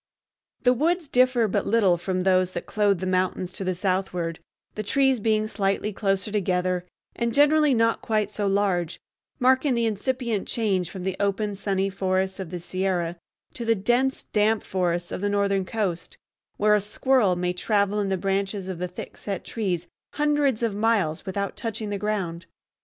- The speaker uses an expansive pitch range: No, average, 3.4 semitones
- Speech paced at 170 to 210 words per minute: Yes, average, 175 wpm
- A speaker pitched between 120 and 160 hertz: No, high, 200 Hz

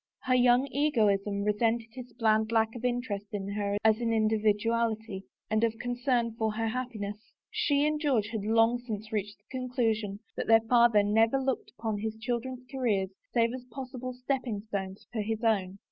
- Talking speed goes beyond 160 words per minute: Yes, average, 175 wpm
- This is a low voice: No, high, 225 Hz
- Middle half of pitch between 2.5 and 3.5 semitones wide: Yes, average, 2.8 semitones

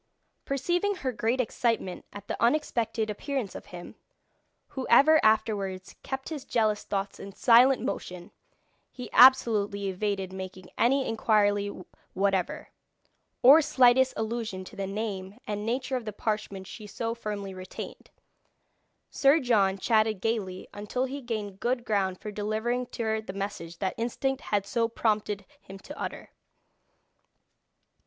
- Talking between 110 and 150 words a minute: Yes, average, 140 wpm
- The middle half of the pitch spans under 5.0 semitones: Yes, average, 3.8 semitones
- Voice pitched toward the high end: Yes, high, 215 Hz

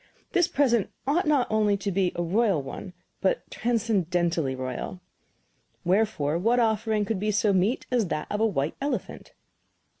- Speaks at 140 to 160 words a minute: Yes, average, 155 wpm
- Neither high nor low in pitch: No, high, 205 Hz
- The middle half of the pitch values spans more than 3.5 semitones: Yes, average, 4.7 semitones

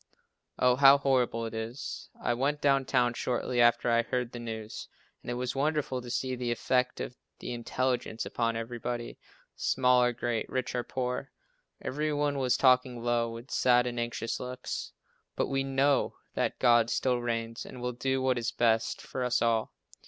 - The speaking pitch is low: Yes, low, 125 Hz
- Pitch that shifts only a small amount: Yes, narrow, 1.7 semitones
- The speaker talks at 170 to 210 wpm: Yes, average, 180 wpm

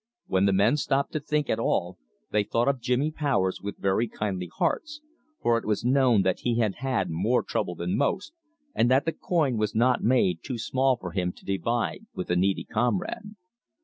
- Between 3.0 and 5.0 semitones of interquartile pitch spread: No, wide, 5.6 semitones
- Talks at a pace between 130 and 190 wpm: No, average, 200 wpm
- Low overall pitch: Yes, low, 115 Hz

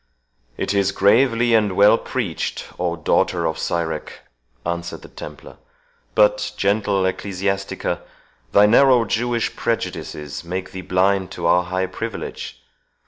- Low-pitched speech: Yes, very low, 95 Hz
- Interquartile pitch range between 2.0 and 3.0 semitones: No, average, 4.0 semitones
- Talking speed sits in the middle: No, slow, 125 wpm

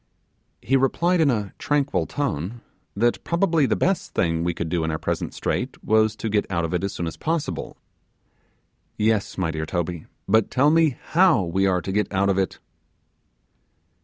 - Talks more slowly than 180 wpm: No, average, 185 wpm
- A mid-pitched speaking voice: No, low, 105 Hz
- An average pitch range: No, wide, 8.2 semitones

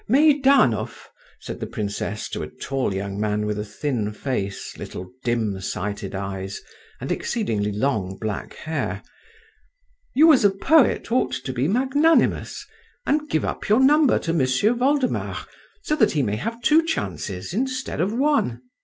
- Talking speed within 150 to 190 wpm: Yes, average, 155 wpm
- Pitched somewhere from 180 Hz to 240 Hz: No, medium, 140 Hz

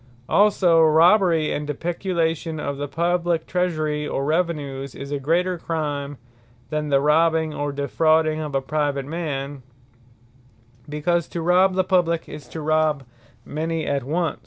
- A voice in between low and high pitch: Yes, medium, 155 Hz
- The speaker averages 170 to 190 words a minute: No, average, 145 wpm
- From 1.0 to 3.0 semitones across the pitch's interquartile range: Yes, average, 2.7 semitones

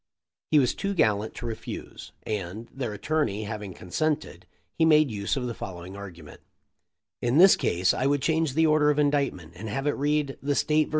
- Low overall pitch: Yes, low, 130 Hz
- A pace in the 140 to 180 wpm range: No, average, 190 wpm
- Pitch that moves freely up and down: Yes, wide, 6.7 semitones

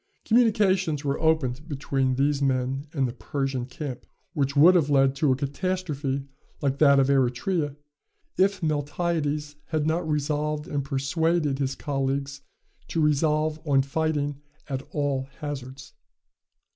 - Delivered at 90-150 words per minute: Yes, slow, 135 wpm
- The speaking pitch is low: No, medium, 145 Hz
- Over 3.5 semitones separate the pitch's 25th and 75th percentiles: No, narrow, 2.5 semitones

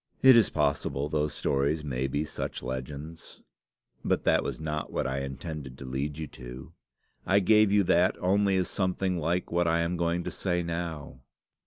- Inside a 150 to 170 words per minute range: No, average, 180 wpm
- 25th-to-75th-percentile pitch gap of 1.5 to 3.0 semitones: No, average, 4.2 semitones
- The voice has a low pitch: Yes, very low, 80 Hz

